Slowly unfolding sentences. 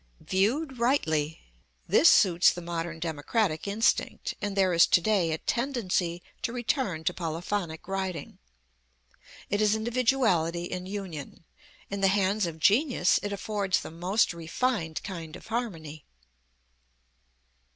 Yes: slow, 130 wpm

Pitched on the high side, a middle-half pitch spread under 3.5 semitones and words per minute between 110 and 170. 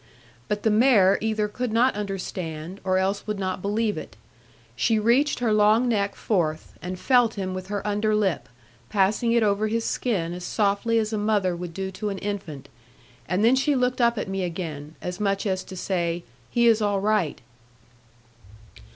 No: high, 205 Hz; average, 3.0 semitones; average, 185 wpm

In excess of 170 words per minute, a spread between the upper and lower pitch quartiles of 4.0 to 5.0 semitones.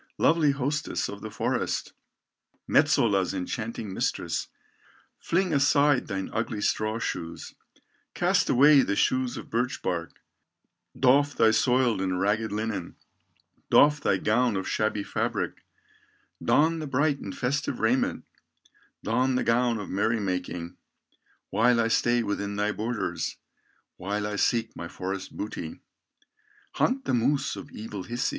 No: slow, 135 wpm; average, 4.3 semitones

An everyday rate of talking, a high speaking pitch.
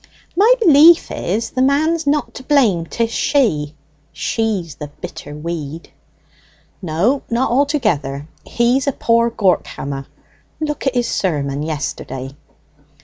No: slow, 125 wpm; high, 225 Hz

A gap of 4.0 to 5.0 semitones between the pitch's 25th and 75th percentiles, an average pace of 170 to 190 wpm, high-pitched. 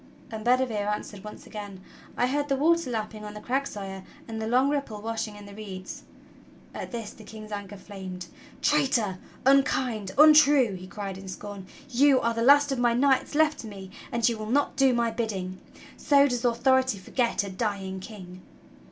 Yes: average, 4.4 semitones; average, 185 wpm; high, 225 Hz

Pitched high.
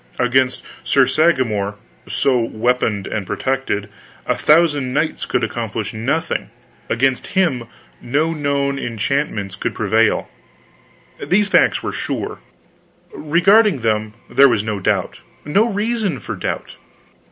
No: low, 130 Hz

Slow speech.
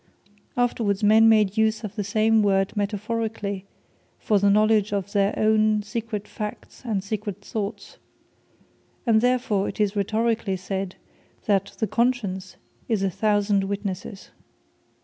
Yes: slow, 130 wpm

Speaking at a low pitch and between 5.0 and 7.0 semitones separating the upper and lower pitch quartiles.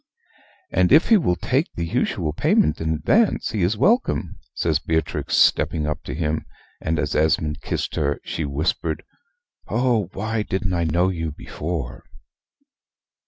Yes: very low, 85 Hz; wide, 5.6 semitones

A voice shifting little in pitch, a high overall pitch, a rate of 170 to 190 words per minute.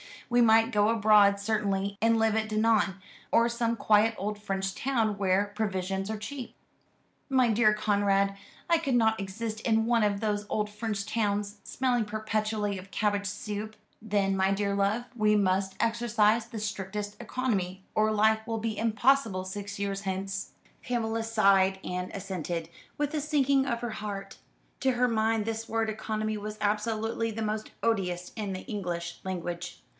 No: narrow, 2.2 semitones; high, 215 Hz; average, 160 wpm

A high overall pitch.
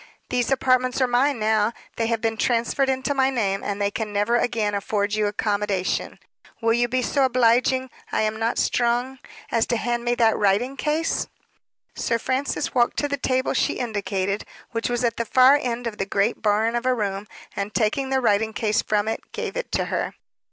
Yes: high, 235 Hz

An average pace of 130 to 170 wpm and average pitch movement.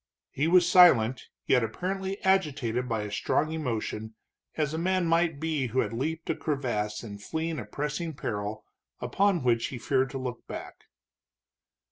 No: average, 160 wpm; wide, 6.1 semitones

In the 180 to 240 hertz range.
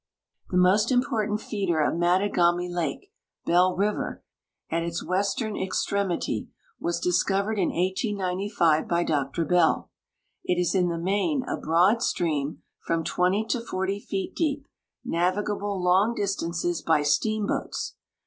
Yes: medium, 185 Hz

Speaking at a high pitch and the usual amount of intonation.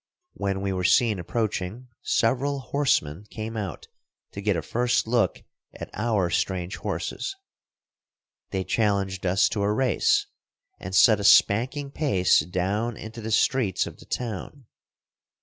No: low, 105 Hz; average, 4.0 semitones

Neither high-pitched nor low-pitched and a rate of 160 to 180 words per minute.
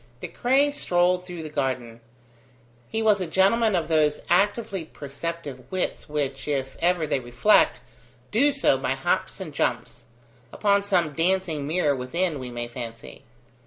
No: medium, 165 Hz; average, 150 wpm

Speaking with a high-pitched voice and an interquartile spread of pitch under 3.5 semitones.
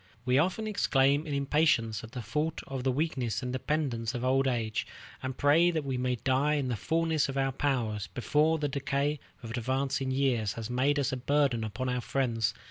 No: low, 135 Hz; average, 3.0 semitones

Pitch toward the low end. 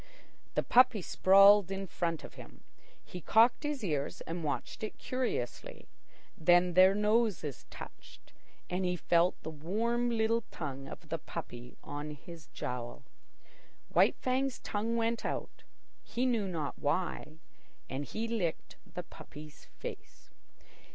No: medium, 185 Hz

